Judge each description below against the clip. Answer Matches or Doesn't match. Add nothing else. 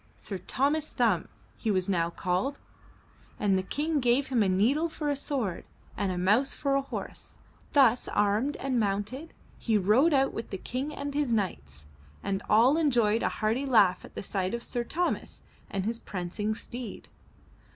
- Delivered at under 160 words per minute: Doesn't match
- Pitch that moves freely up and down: Matches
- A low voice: Doesn't match